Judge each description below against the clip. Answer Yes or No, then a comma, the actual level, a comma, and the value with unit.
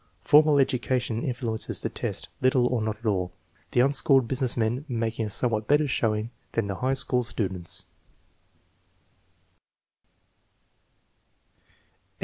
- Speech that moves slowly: Yes, slow, 120 wpm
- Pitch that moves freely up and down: No, average, 3.0 semitones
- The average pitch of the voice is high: No, low, 120 Hz